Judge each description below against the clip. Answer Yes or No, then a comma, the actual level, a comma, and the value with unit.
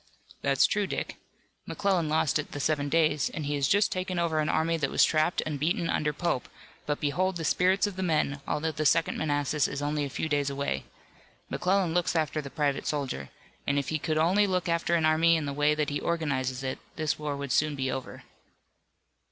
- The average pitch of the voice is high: No, medium, 155 Hz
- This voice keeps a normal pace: No, fast, 215 wpm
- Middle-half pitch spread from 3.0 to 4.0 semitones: No, narrow, 2.6 semitones